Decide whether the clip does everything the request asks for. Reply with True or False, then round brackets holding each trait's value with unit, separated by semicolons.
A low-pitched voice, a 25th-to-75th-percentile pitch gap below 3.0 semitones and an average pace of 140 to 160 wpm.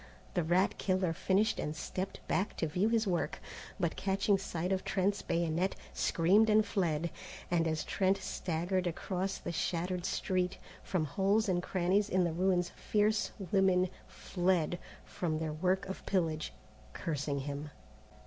False (180 Hz; 2.6 semitones; 150 wpm)